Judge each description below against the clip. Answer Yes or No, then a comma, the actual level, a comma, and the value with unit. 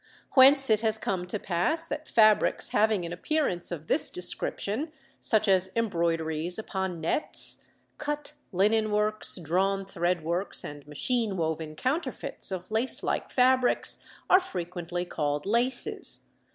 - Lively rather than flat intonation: No, average, 5.0 semitones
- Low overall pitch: No, high, 195 Hz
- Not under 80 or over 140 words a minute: Yes, slow, 135 wpm